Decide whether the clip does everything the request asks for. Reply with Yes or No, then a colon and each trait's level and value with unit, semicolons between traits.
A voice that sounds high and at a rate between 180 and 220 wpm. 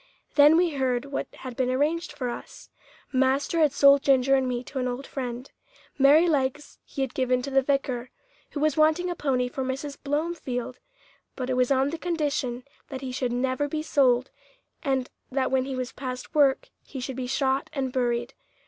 Yes: very high, 265 Hz; average, 190 wpm